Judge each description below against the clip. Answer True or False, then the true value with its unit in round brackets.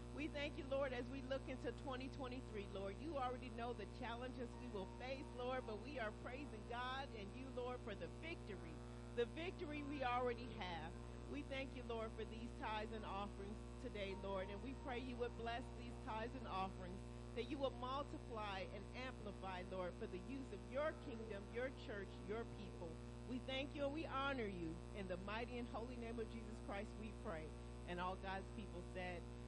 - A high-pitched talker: False (85 Hz)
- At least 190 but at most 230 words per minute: True (195 wpm)